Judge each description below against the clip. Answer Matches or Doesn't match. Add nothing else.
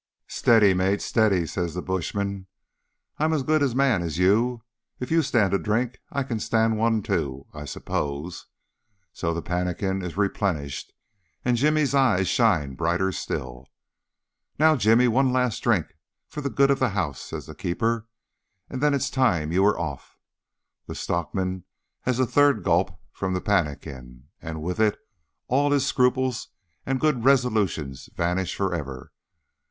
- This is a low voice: Matches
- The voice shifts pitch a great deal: Matches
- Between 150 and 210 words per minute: Matches